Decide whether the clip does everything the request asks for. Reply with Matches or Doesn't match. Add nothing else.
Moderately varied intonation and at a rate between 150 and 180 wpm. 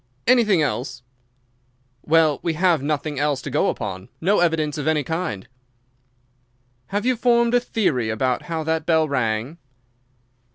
Doesn't match